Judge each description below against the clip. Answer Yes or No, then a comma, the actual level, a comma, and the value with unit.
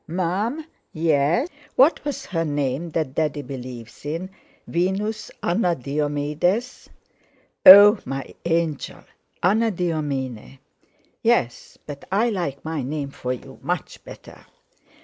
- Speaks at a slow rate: Yes, slow, 110 wpm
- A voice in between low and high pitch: Yes, medium, 165 Hz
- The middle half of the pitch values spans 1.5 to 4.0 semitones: No, wide, 5.6 semitones